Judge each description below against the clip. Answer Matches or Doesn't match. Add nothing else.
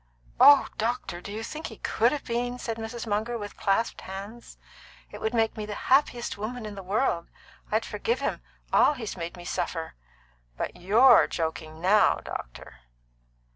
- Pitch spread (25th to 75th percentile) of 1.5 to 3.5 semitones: Doesn't match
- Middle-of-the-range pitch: Doesn't match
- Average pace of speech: Matches